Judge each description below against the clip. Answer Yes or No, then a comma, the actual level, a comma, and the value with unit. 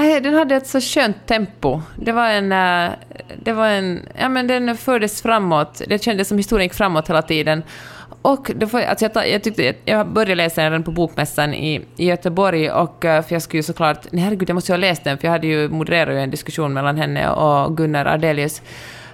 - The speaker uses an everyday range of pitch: No, wide, 5.9 semitones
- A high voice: No, medium, 175 Hz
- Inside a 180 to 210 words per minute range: Yes, average, 200 wpm